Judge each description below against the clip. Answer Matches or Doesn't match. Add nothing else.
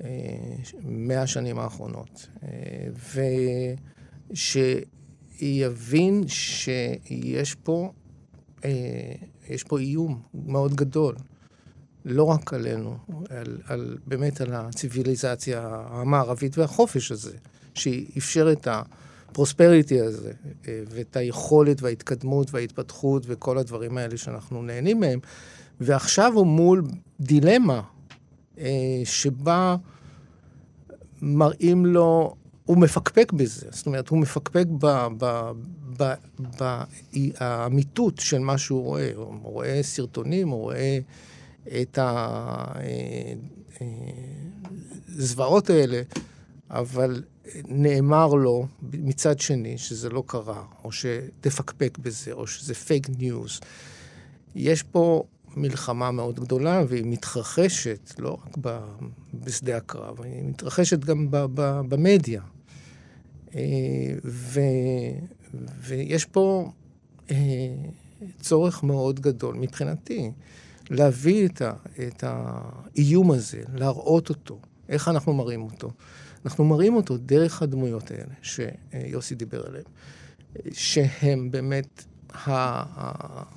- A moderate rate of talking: Doesn't match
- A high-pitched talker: Doesn't match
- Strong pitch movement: Doesn't match